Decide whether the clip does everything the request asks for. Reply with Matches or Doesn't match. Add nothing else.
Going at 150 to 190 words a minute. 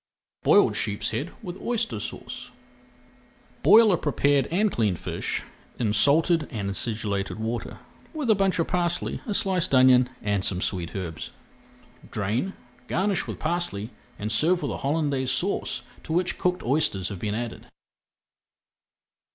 Doesn't match